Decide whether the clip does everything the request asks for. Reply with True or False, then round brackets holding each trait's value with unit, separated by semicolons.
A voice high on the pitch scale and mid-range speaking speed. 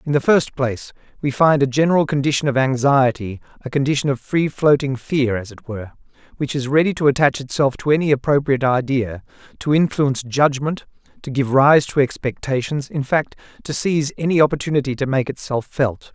False (135 Hz; 180 wpm)